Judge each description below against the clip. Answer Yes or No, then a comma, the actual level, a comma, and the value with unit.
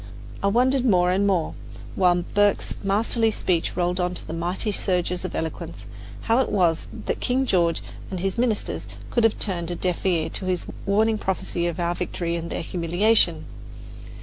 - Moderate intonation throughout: Yes, average, 3.5 semitones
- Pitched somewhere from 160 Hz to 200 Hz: Yes, medium, 185 Hz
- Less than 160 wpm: No, average, 175 wpm